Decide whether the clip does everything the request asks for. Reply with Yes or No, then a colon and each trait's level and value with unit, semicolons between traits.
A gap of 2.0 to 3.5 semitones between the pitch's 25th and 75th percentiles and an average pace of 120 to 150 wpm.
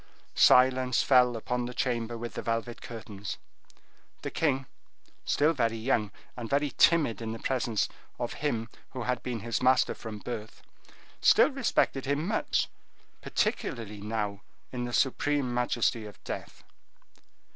Yes: narrow, 2.6 semitones; average, 145 wpm